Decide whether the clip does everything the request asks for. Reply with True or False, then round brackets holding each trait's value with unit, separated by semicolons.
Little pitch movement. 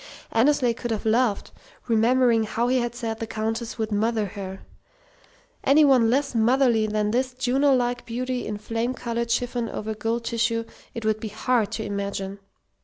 True (2.2 semitones)